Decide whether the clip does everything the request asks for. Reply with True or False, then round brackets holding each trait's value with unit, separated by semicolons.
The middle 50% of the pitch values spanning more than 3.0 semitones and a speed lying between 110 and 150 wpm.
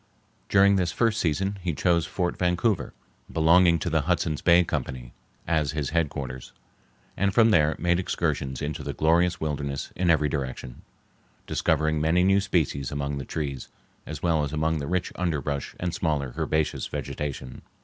False (3.6 semitones; 160 wpm)